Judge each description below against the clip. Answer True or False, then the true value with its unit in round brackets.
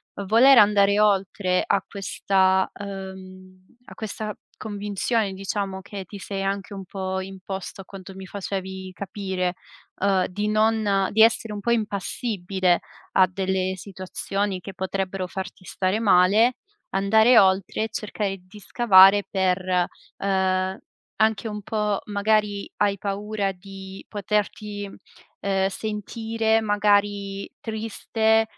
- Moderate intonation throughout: False (1.8 semitones)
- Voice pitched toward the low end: False (200 Hz)